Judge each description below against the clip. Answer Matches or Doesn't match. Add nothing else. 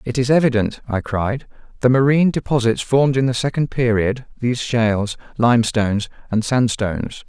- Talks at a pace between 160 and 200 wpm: Doesn't match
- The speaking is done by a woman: Doesn't match